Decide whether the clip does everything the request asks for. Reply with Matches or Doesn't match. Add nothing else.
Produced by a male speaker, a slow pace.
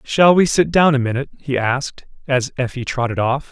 Doesn't match